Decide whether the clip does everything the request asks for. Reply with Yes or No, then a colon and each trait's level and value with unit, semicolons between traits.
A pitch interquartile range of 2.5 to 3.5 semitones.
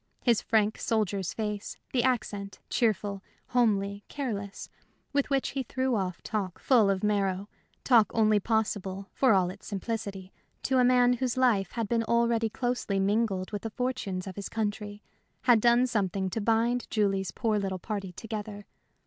Yes: average, 3.1 semitones